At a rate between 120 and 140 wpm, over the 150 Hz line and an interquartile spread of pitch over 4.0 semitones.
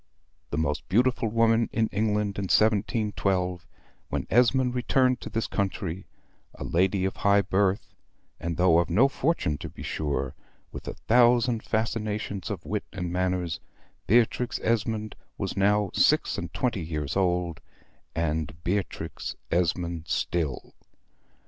No: slow, 135 wpm; low, 100 Hz; average, 4.4 semitones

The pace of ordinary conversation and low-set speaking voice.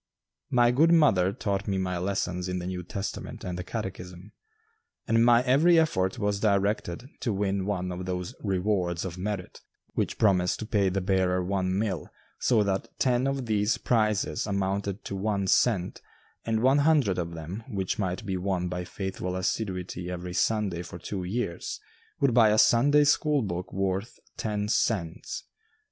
Yes: average, 165 wpm; low, 100 Hz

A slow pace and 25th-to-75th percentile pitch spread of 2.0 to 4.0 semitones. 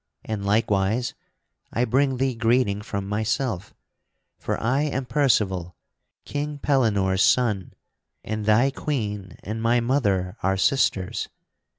No: slow, 115 wpm; average, 4.6 semitones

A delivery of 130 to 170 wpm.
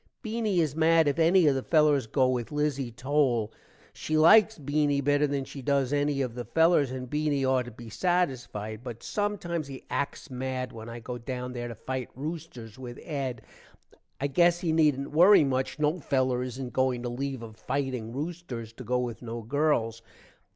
No: average, 185 wpm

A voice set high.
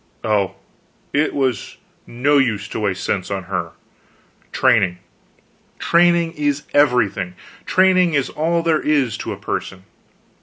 No: low, 135 Hz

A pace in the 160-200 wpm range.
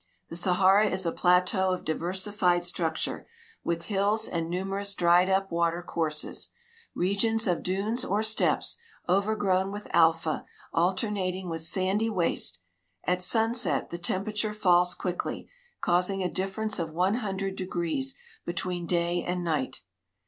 No: slow, 135 wpm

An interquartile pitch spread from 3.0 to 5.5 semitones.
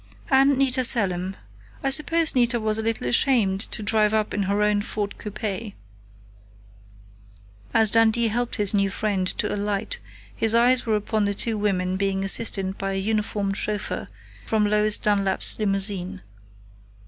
No: narrow, 2.4 semitones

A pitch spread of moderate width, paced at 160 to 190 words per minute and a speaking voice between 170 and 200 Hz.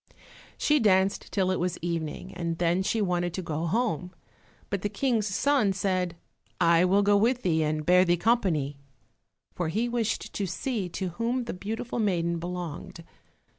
Yes: average, 3.9 semitones; average, 170 wpm; medium, 185 Hz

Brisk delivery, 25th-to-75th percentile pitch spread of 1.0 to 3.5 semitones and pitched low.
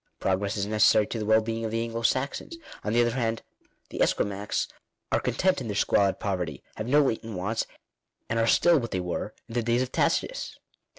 Yes: fast, 210 wpm; narrow, 2.4 semitones; low, 115 Hz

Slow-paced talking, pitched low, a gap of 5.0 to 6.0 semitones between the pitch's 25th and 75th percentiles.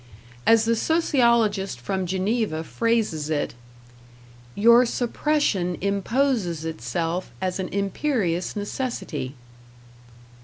No: slow, 85 wpm; high, 200 Hz; average, 5.3 semitones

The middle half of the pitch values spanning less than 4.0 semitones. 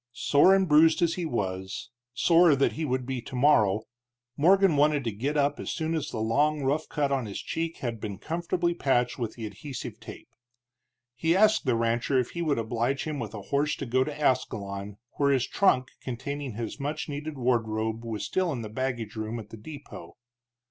No: average, 5.0 semitones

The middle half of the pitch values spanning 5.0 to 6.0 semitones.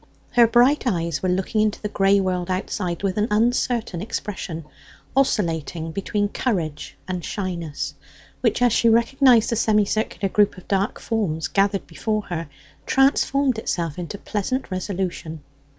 No: average, 4.2 semitones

